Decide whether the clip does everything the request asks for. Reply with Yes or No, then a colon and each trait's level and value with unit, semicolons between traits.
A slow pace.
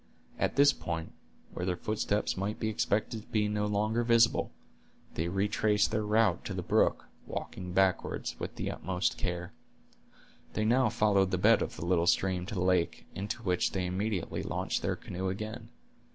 No: average, 175 wpm